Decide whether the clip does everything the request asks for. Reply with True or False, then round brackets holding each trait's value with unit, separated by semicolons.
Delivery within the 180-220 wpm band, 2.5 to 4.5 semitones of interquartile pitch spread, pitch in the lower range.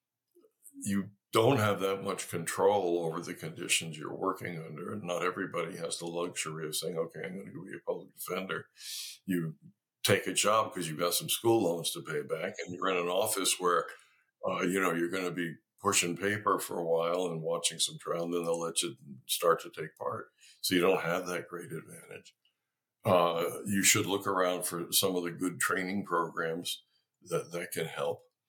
True (200 wpm; 3.8 semitones; 90 Hz)